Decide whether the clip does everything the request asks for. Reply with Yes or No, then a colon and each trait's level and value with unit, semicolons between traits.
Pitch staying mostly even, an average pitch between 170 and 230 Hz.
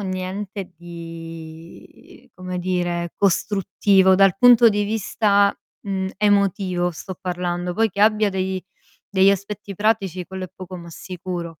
Yes: narrow, 2.2 semitones; high, 190 Hz